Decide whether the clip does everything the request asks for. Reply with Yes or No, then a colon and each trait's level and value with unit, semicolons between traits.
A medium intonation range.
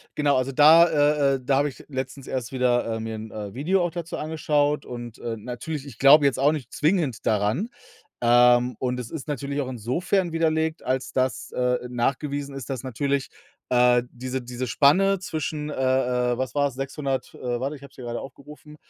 Yes: average, 3.2 semitones